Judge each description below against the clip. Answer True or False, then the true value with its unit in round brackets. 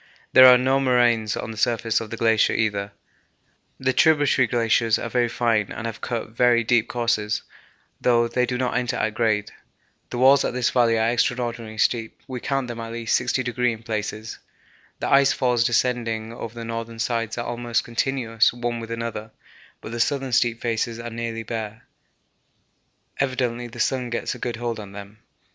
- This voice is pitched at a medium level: False (115 Hz)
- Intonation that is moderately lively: False (1.5 semitones)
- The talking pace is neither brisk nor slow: True (180 wpm)